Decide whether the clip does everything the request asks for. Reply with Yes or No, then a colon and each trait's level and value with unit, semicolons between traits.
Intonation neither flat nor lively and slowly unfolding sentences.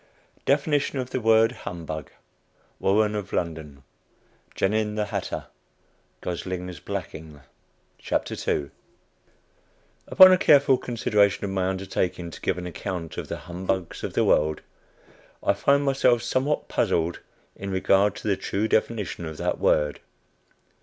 Yes: average, 5.0 semitones; slow, 125 wpm